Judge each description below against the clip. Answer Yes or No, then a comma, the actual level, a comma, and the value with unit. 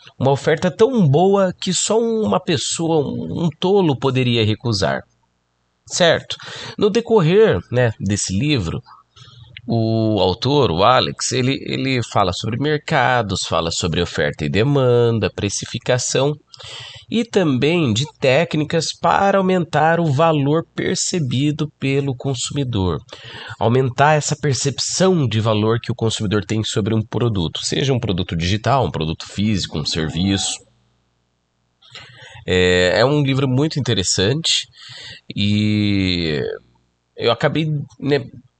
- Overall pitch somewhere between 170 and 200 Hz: No, low, 125 Hz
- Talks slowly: Yes, slow, 115 wpm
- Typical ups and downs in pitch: No, wide, 6.6 semitones